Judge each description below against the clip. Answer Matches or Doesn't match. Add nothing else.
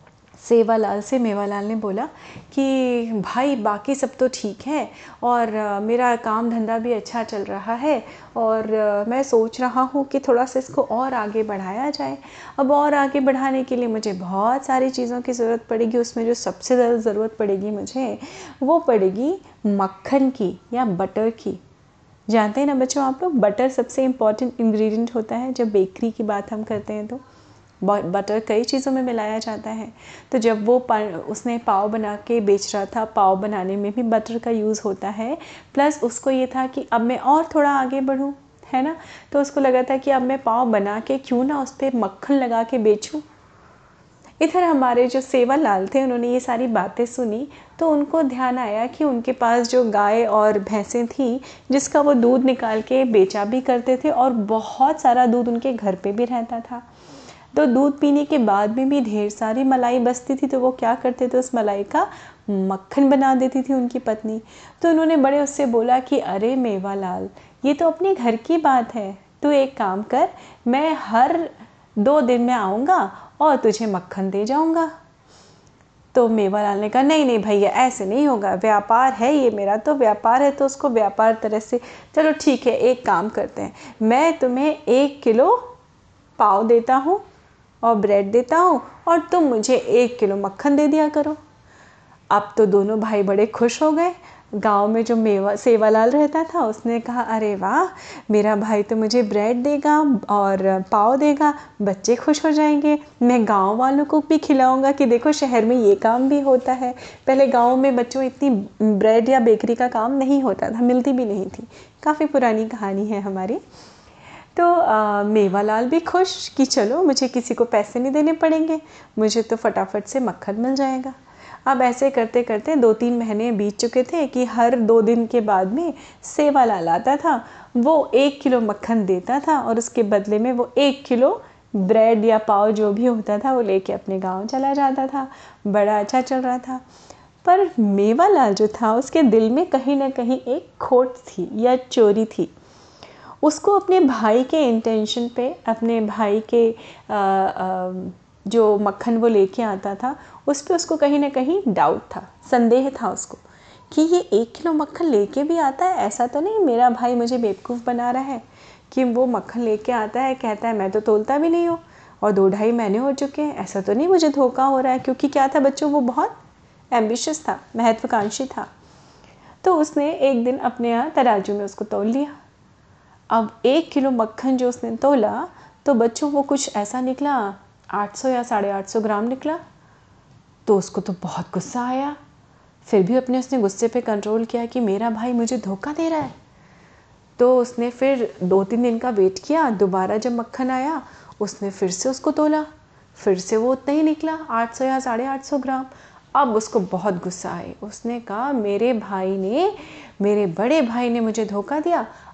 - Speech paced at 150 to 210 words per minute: Matches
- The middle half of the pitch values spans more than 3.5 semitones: Matches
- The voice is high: Matches